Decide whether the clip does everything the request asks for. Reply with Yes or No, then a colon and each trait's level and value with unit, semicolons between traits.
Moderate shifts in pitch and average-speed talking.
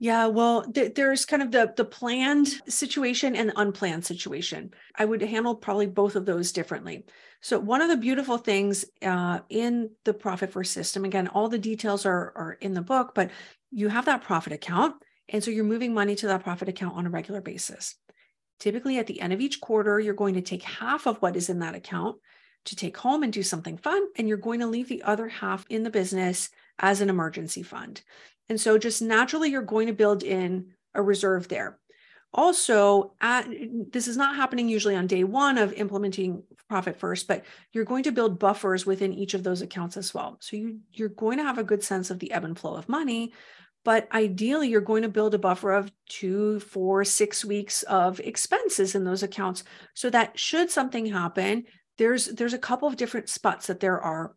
No: average, 3.5 semitones; fast, 210 wpm